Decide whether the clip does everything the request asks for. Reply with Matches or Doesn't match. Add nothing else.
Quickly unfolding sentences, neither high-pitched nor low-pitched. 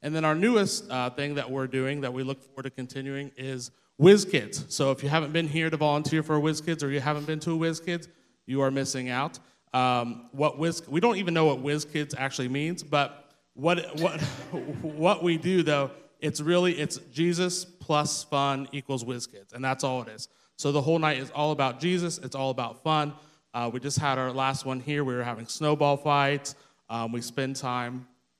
Matches